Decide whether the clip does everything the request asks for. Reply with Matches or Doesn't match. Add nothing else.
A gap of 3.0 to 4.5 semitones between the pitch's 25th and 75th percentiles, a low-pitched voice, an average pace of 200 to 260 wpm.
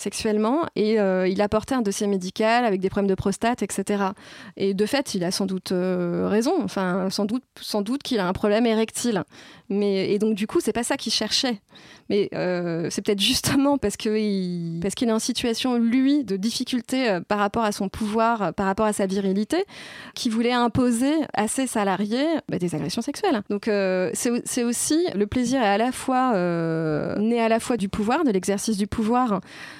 Doesn't match